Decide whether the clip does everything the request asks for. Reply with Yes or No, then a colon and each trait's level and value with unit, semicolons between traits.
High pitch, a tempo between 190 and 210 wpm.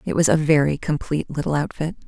No: medium, 150 Hz; average, 200 wpm